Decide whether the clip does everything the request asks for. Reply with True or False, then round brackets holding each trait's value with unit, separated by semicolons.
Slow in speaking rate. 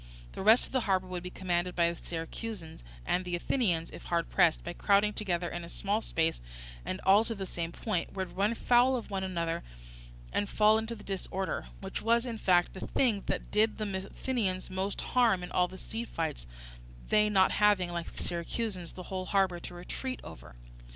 False (200 wpm)